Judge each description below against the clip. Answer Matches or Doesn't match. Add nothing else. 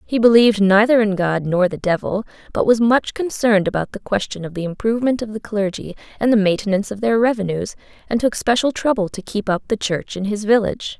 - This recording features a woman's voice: Matches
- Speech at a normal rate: Doesn't match